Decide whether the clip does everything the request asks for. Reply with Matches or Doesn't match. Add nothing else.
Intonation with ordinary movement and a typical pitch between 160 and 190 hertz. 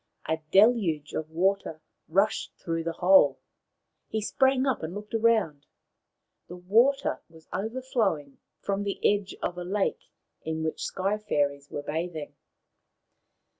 Matches